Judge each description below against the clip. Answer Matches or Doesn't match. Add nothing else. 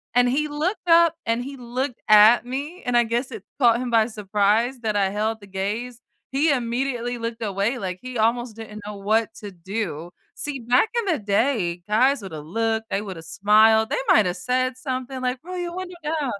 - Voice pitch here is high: Matches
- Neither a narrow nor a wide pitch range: Matches